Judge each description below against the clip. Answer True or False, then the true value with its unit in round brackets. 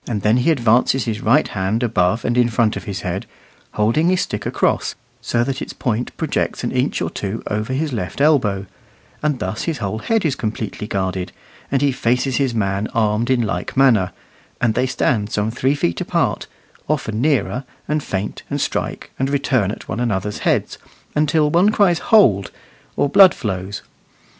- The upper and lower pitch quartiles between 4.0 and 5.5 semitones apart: True (4.8 semitones)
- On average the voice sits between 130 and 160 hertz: False (120 Hz)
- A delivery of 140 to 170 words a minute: False (180 wpm)